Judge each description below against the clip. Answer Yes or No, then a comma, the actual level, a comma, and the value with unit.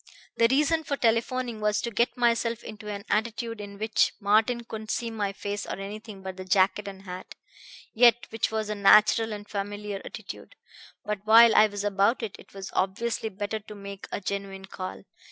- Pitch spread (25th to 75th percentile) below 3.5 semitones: Yes, narrow, 2.4 semitones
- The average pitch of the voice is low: No, high, 210 Hz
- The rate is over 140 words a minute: Yes, average, 190 wpm